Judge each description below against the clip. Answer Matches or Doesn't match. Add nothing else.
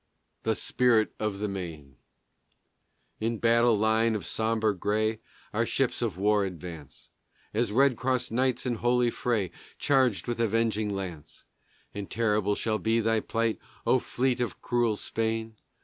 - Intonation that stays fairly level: Matches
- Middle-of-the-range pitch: Doesn't match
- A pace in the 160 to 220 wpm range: Doesn't match